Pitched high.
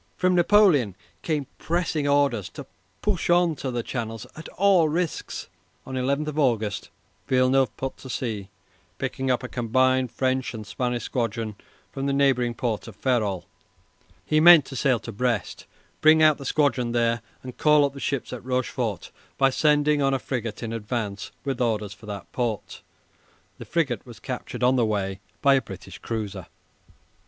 No: low, 130 Hz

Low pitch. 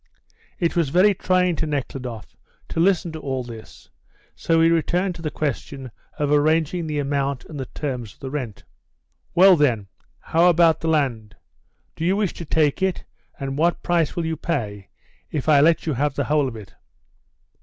No: medium, 150 Hz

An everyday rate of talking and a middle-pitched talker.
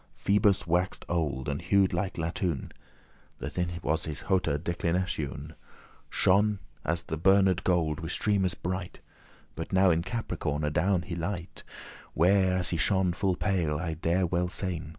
No: average, 155 wpm; very low, 90 Hz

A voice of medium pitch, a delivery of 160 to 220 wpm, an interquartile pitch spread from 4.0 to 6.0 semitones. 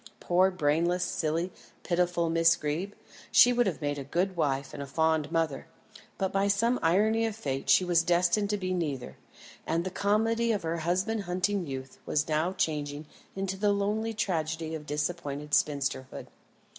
Yes: medium, 170 Hz; average, 170 wpm; average, 4.4 semitones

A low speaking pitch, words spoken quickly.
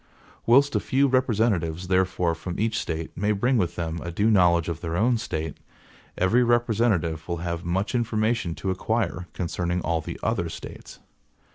No: very low, 95 Hz; average, 165 wpm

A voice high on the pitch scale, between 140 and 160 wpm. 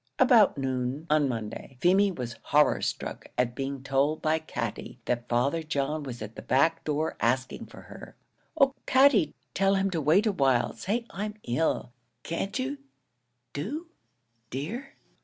No: medium, 150 Hz; average, 150 wpm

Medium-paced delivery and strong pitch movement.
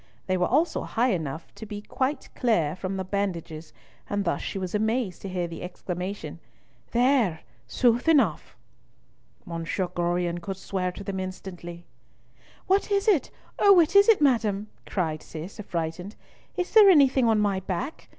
Yes: average, 160 wpm; wide, 6.0 semitones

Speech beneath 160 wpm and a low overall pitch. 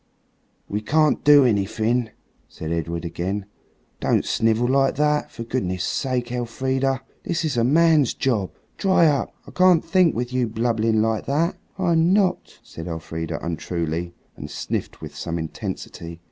Yes: average, 145 wpm; low, 120 Hz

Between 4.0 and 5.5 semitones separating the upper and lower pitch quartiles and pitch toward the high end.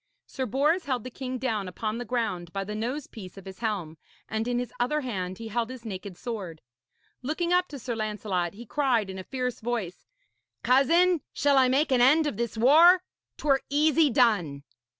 Yes: average, 4.9 semitones; high, 240 Hz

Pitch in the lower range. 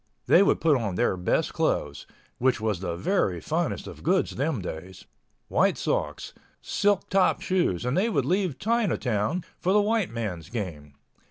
Yes: low, 125 Hz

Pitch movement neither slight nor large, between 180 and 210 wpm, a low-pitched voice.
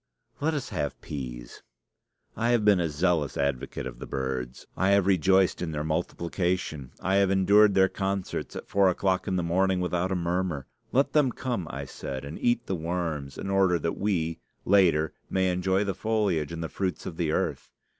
Yes: average, 3.6 semitones; average, 190 wpm; very low, 90 Hz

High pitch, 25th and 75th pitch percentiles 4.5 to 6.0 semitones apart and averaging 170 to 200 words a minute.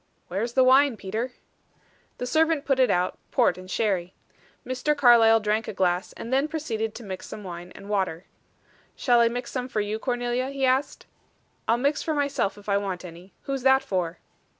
Yes: high, 230 Hz; average, 5.1 semitones; average, 195 wpm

